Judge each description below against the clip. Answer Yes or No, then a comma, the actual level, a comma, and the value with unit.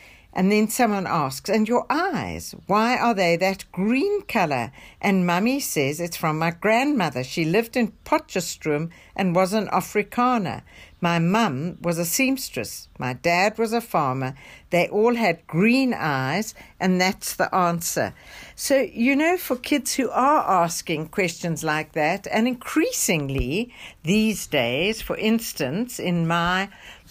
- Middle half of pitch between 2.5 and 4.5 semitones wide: No, wide, 5.5 semitones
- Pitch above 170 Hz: Yes, high, 190 Hz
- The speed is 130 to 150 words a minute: Yes, average, 145 wpm